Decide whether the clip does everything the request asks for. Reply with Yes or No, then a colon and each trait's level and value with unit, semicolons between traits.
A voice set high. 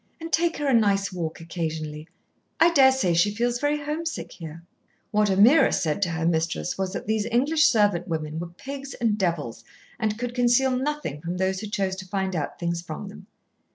Yes: high, 195 Hz